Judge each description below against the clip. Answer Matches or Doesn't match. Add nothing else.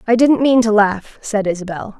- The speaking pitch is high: Matches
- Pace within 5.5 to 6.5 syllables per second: Doesn't match